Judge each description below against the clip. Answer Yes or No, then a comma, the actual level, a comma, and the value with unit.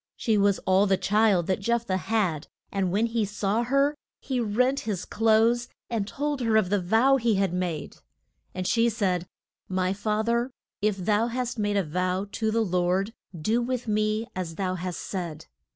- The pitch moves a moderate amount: Yes, average, 3.8 semitones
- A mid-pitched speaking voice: No, high, 210 Hz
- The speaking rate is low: No, average, 185 wpm